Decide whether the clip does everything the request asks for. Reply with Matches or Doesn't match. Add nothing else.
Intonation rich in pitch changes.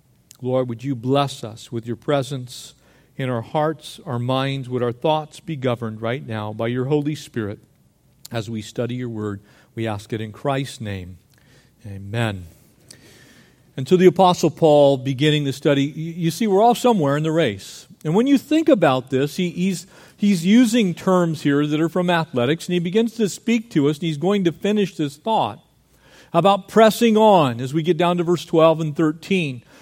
Matches